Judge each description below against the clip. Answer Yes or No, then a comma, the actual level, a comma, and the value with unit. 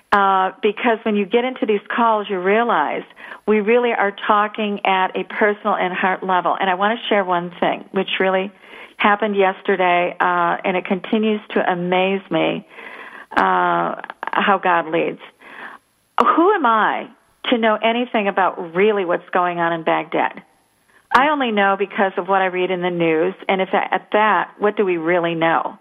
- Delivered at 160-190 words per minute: Yes, average, 175 wpm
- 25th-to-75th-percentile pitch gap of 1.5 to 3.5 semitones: Yes, average, 2.8 semitones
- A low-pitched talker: No, high, 195 Hz